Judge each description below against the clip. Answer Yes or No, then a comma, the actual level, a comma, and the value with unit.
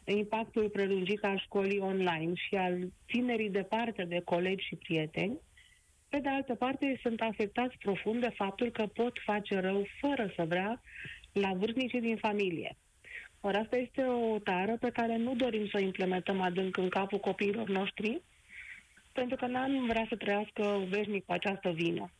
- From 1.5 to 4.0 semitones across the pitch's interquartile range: Yes, average, 3.5 semitones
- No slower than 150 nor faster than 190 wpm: Yes, average, 160 wpm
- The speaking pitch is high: Yes, high, 205 Hz